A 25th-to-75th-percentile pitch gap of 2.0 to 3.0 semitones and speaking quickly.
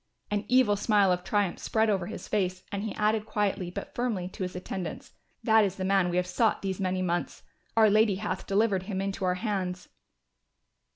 No: narrow, 2.4 semitones; average, 195 wpm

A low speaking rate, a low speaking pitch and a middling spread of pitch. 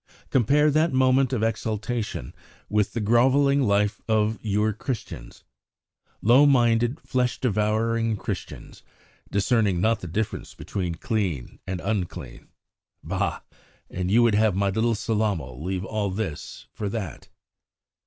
Yes: slow, 125 wpm; low, 110 Hz; average, 3.0 semitones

